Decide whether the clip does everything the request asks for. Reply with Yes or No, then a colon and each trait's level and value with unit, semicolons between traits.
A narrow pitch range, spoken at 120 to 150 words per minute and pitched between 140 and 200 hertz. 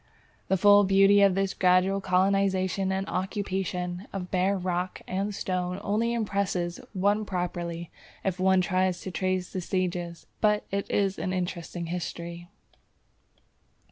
Yes: narrow, 1.5 semitones; average, 140 wpm; medium, 185 Hz